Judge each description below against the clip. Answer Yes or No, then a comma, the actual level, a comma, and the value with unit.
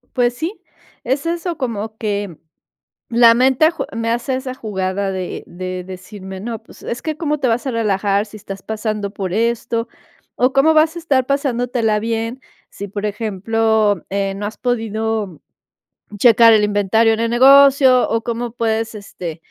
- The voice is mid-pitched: No, high, 225 Hz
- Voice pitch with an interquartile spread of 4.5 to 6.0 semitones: No, average, 3.4 semitones